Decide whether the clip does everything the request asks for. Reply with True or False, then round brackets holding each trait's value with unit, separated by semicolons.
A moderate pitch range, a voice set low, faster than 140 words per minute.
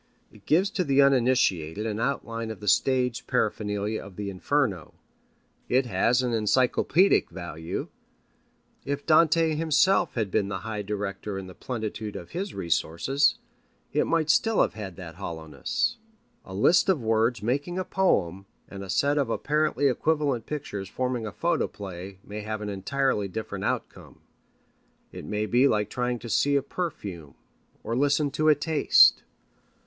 False (6.1 semitones; 115 Hz; 155 wpm)